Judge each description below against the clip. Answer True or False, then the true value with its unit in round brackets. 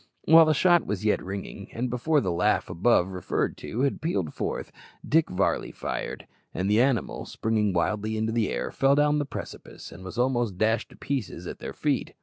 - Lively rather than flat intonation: True (6.0 semitones)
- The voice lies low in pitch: True (110 Hz)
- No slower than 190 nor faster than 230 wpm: True (195 wpm)